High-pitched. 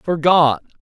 No: medium, 155 Hz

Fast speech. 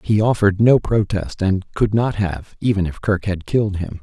Yes: fast, 210 wpm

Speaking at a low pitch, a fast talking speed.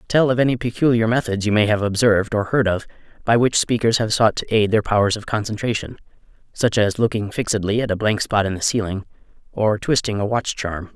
Yes: low, 110 Hz; fast, 215 wpm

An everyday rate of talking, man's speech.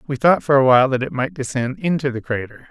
No: fast, 265 wpm; male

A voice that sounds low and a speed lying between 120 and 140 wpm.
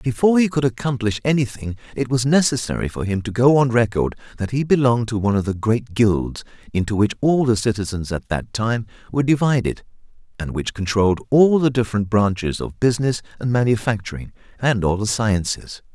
No: low, 115 Hz; average, 180 wpm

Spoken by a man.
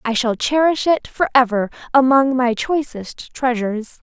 No: female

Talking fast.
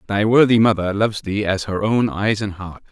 Yes: fast, 225 wpm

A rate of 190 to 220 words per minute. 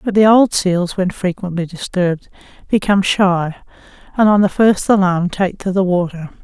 No: average, 170 wpm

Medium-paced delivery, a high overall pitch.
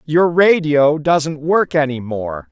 No: average, 145 wpm; medium, 150 Hz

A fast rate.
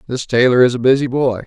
Yes: fast, 245 wpm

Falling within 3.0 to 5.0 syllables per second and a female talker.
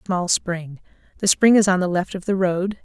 Yes: 4.8 syllables/s; female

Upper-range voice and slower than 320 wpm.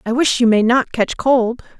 Yes: high, 240 Hz; fast, 235 wpm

